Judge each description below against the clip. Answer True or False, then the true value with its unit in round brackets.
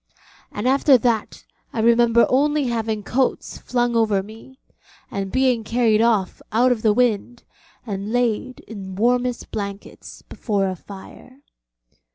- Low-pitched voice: False (230 Hz)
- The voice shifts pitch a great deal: False (3.0 semitones)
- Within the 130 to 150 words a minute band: True (135 wpm)